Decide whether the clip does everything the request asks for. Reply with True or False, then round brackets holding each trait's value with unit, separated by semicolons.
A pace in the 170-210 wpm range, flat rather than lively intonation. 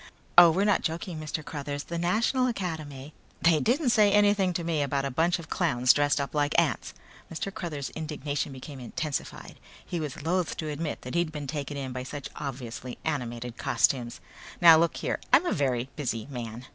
False (190 wpm; 3.9 semitones)